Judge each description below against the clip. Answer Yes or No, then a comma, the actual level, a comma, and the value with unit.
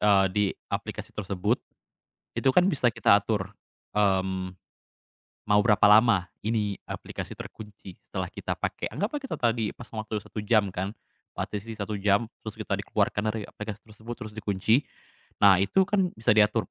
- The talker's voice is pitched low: Yes, low, 105 Hz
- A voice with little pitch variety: Yes, narrow, 2.2 semitones